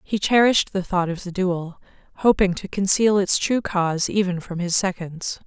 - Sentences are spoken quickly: No, average, 185 wpm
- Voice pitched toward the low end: No, high, 190 Hz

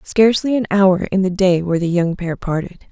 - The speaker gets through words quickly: Yes, fast, 225 wpm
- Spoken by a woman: Yes, female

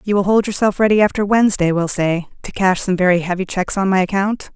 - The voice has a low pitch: No, high, 190 Hz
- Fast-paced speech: Yes, fast, 235 wpm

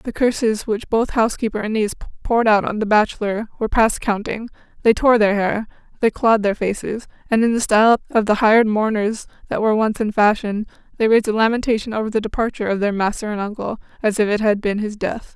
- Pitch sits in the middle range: No, high, 215 Hz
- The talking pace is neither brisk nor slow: No, fast, 215 wpm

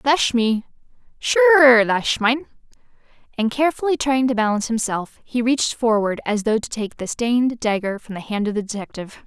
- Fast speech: No, average, 170 wpm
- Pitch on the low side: No, high, 235 Hz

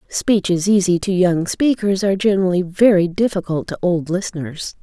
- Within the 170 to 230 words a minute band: No, average, 150 wpm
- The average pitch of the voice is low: No, medium, 185 Hz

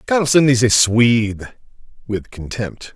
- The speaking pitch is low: Yes, low, 120 Hz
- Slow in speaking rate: Yes, slow, 120 wpm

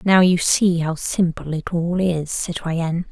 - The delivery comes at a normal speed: Yes, average, 175 wpm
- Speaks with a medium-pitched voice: Yes, medium, 170 Hz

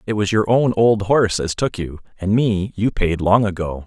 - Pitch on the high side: No, low, 100 Hz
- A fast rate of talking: Yes, fast, 235 wpm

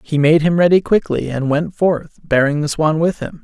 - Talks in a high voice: No, medium, 160 Hz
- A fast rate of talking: Yes, fast, 225 wpm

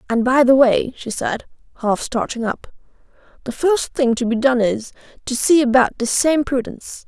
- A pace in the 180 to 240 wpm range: Yes, average, 185 wpm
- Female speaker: Yes, female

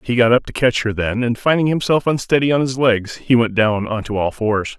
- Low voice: Yes, low, 120 Hz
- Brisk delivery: Yes, fast, 265 wpm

